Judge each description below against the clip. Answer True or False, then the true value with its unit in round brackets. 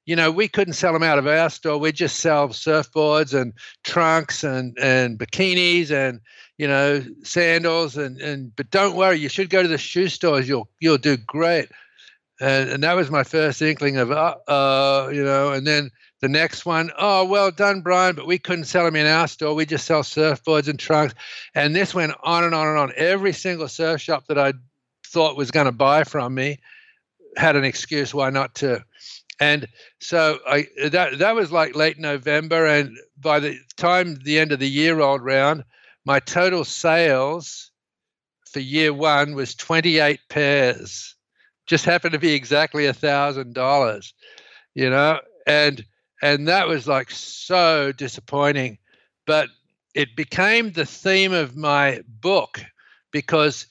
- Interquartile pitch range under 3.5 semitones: True (2.9 semitones)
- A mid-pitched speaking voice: True (150 Hz)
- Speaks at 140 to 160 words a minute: False (175 wpm)